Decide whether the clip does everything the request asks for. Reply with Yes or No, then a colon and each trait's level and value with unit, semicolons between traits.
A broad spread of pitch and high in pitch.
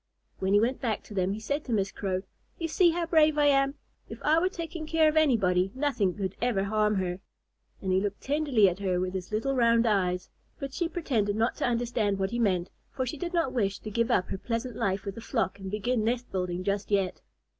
Yes: wide, 6.0 semitones; high, 220 Hz